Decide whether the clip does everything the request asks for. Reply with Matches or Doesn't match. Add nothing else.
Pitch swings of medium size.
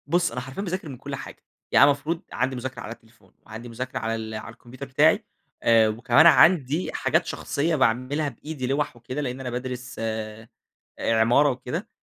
Matches